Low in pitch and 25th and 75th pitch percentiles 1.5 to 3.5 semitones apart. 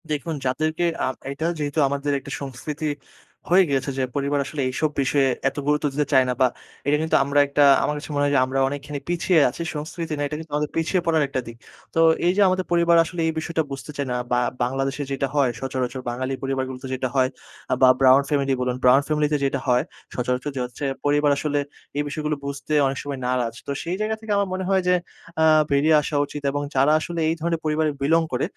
No: medium, 145 Hz; average, 2.8 semitones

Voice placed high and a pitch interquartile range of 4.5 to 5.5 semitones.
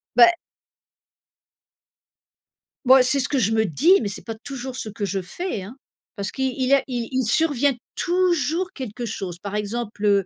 Yes: high, 245 Hz; average, 5.0 semitones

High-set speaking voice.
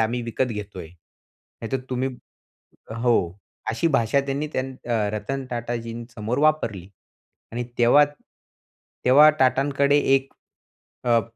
No: low, 120 Hz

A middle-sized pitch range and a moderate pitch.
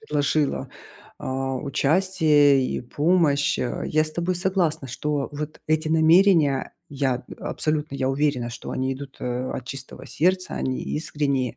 Yes: average, 3.0 semitones; medium, 145 Hz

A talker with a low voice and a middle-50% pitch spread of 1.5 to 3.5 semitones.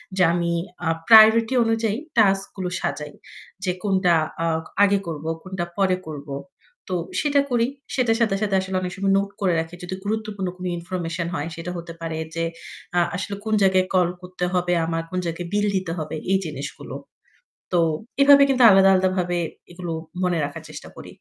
No: medium, 185 Hz; average, 2.9 semitones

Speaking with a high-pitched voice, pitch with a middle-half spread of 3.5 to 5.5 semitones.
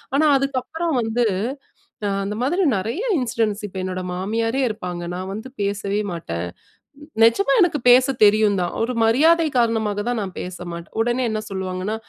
Yes: high, 220 Hz; average, 4.5 semitones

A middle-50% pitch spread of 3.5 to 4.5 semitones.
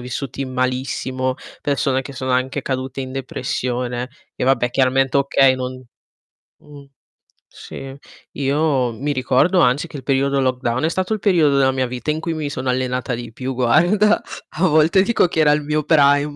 No: narrow, 2.6 semitones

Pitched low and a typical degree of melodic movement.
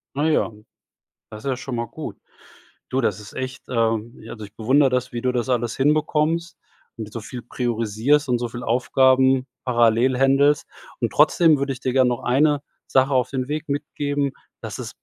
Yes: low, 130 Hz; average, 3.1 semitones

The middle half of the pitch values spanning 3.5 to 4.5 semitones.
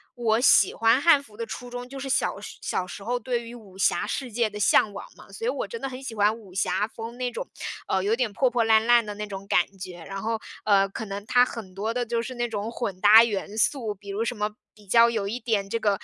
No: average, 3.0 semitones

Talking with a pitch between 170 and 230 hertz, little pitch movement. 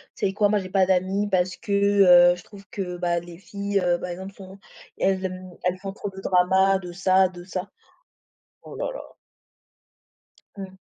Yes: high, 190 Hz; narrow, 1.4 semitones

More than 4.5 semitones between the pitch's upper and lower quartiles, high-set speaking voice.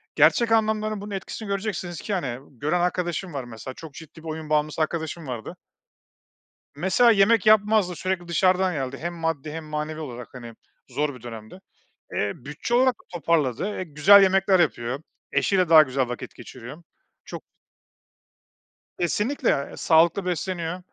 No: average, 5.2 semitones; medium, 165 Hz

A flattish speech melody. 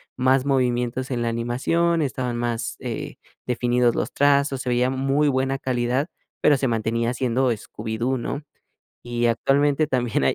Yes: narrow, 2.3 semitones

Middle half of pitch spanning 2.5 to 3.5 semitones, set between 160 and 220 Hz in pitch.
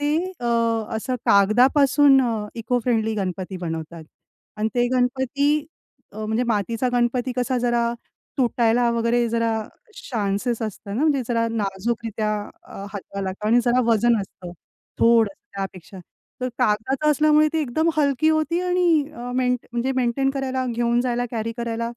No: average, 2.9 semitones; high, 235 Hz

